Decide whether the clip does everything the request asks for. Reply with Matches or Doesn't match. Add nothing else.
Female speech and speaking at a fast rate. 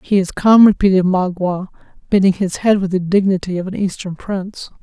Doesn't match